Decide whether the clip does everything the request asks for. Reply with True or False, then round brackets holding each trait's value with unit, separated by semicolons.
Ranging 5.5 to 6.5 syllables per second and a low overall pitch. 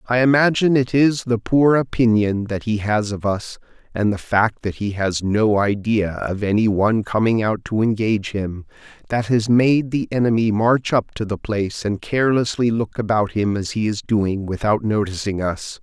False (4.8 syllables/s; 110 Hz)